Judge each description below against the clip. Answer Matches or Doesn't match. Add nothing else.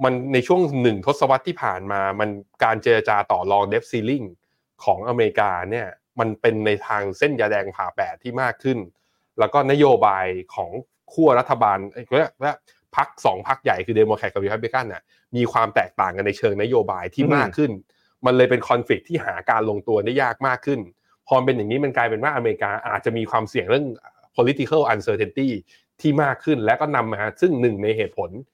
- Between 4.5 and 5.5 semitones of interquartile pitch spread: Matches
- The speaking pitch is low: Matches